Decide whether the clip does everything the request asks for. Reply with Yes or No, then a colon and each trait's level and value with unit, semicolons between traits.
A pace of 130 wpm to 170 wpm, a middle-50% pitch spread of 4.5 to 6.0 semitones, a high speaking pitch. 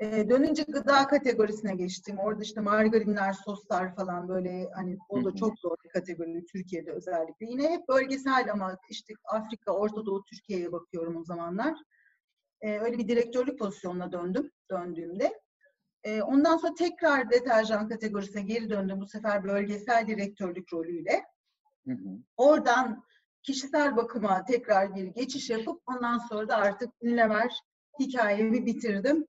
Yes: average, 135 wpm; average, 4.9 semitones; high, 215 Hz